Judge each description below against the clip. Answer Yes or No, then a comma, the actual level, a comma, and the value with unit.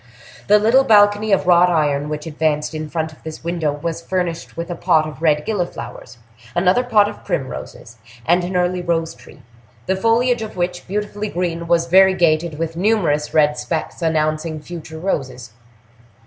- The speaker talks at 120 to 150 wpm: No, average, 165 wpm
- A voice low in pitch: No, medium, 170 Hz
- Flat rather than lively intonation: No, average, 3.4 semitones